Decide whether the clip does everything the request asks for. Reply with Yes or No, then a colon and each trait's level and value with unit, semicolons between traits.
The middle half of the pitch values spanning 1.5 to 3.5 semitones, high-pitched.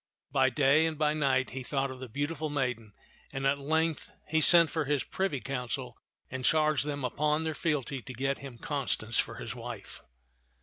No: average, 2.7 semitones; medium, 140 Hz